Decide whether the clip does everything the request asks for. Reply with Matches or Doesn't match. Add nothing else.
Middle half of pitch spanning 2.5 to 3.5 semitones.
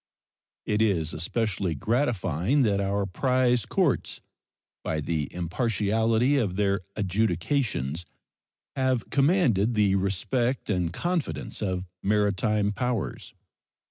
Doesn't match